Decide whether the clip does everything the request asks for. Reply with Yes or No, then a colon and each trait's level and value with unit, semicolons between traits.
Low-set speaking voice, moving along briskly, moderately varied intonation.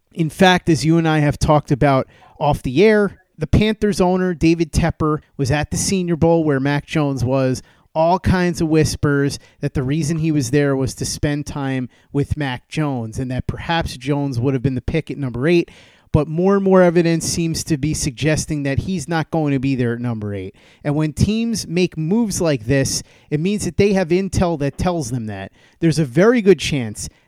No: medium, 150 Hz; fast, 210 wpm; average, 3.7 semitones